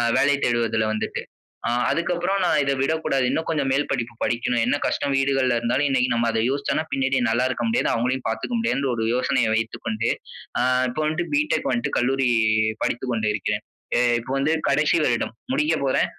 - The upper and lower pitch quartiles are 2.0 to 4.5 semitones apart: Yes, average, 3.7 semitones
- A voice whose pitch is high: No, low, 130 Hz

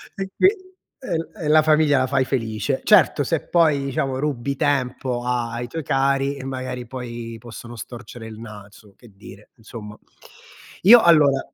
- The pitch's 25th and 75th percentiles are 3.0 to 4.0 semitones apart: Yes, average, 3.7 semitones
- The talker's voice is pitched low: Yes, low, 130 Hz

